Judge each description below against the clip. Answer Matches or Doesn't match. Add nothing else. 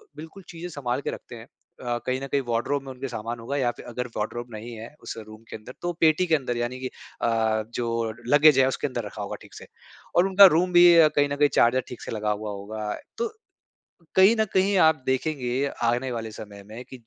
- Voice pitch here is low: Matches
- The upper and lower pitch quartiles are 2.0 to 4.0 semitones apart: Doesn't match